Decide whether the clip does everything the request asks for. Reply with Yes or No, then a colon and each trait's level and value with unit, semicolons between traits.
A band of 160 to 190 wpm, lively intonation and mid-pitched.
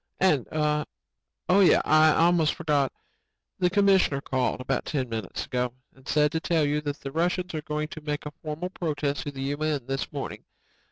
No: average, 180 wpm; average, 2.8 semitones; medium, 150 Hz